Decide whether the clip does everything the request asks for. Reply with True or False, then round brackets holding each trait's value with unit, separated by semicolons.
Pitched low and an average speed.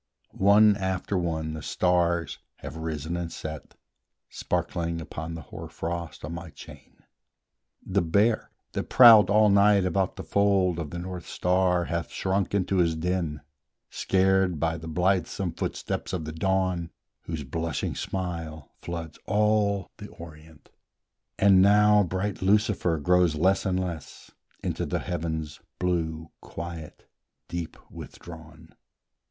False (85 Hz; 130 wpm)